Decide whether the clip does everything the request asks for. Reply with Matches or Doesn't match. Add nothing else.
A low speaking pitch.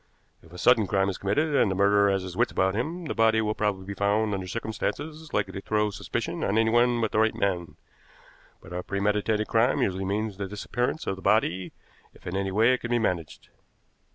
Matches